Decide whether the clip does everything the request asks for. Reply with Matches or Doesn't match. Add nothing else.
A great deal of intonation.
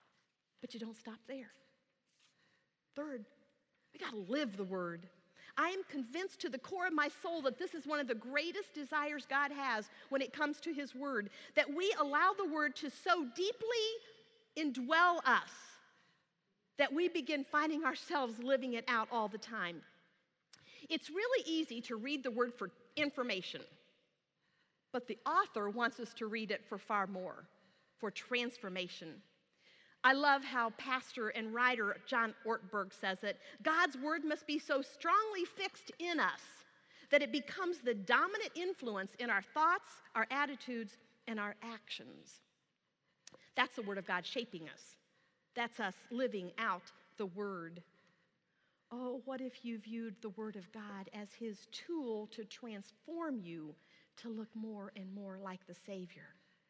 Matches